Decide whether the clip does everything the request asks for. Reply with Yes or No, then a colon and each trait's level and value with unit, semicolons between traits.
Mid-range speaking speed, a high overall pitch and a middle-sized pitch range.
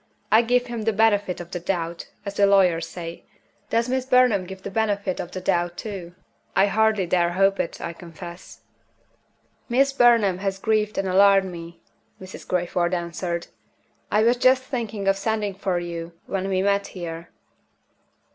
Yes: average, 170 wpm; high, 195 Hz; average, 3.8 semitones